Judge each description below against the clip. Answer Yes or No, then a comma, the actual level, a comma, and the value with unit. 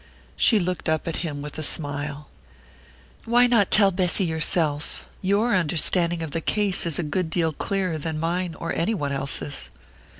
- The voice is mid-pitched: Yes, medium, 165 Hz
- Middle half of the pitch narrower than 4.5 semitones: Yes, average, 3.5 semitones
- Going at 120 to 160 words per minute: No, average, 170 wpm